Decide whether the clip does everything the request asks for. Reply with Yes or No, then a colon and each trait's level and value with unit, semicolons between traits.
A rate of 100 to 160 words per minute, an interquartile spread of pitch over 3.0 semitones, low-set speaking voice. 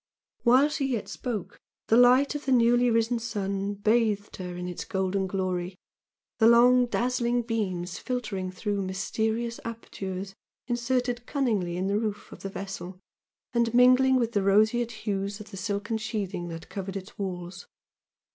No: average, 155 wpm; average, 3.7 semitones; high, 215 Hz